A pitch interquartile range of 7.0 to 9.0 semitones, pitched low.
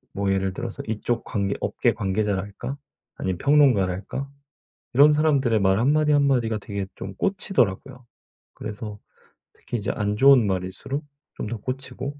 No: wide, 5.6 semitones; low, 115 Hz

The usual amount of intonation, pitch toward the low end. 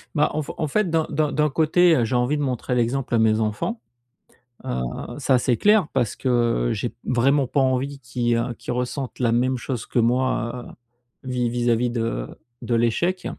Yes: average, 3.4 semitones; low, 125 Hz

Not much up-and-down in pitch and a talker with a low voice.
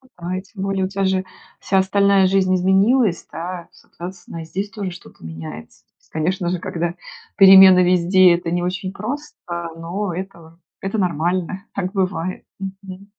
No: narrow, 2.0 semitones; medium, 185 Hz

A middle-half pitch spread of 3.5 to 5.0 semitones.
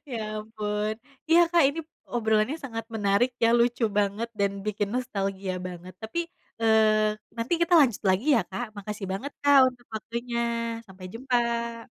No: average, 2.8 semitones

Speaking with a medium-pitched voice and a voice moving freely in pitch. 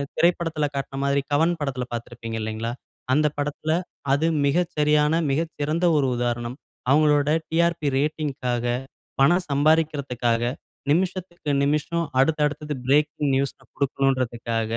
No: medium, 145 Hz; average, 3.4 semitones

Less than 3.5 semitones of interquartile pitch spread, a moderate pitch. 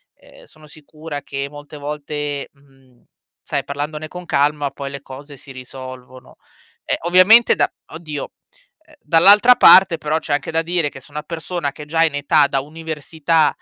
Yes: narrow, 2.5 semitones; medium, 150 Hz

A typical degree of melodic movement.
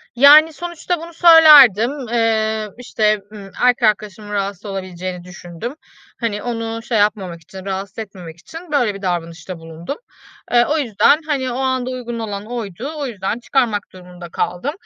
Yes: average, 4.9 semitones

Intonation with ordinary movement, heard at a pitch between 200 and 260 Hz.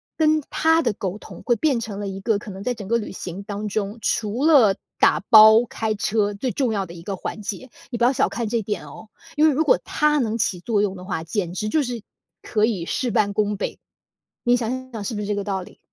Yes: average, 3.4 semitones; high, 215 Hz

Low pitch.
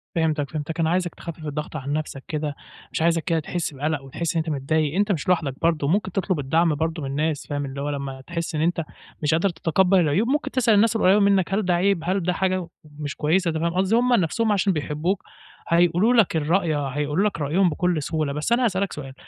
No: medium, 165 Hz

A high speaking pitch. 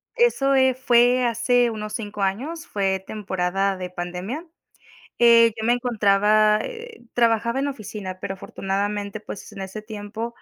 Yes: high, 215 Hz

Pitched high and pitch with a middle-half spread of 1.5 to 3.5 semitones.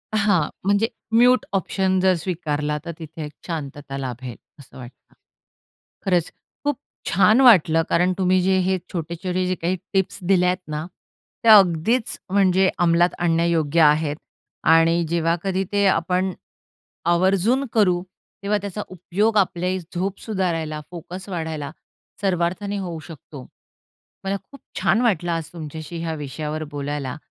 No: medium, 175 Hz; average, 3.2 semitones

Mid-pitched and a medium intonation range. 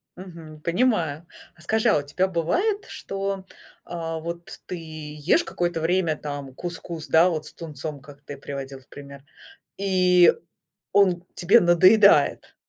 Yes: medium, 170 Hz; average, 3.6 semitones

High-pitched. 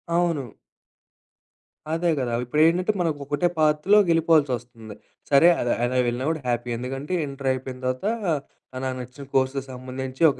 No: low, 135 Hz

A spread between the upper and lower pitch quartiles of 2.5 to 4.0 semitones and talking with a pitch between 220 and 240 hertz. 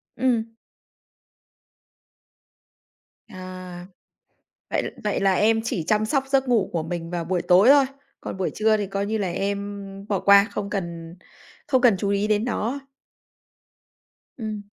No: average, 3.1 semitones; high, 200 Hz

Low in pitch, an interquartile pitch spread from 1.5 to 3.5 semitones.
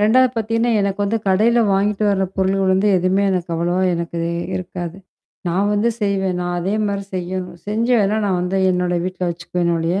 No: high, 190 Hz; narrow, 2.4 semitones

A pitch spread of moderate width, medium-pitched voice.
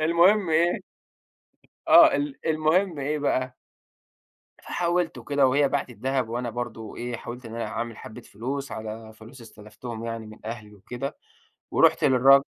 No: average, 4.3 semitones; low, 125 Hz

